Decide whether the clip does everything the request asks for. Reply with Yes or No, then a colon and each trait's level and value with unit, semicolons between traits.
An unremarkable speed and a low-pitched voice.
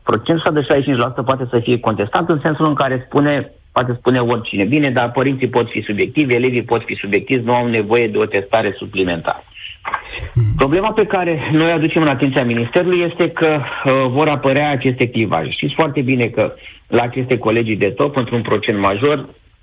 No: fast, 180 wpm; low, 130 Hz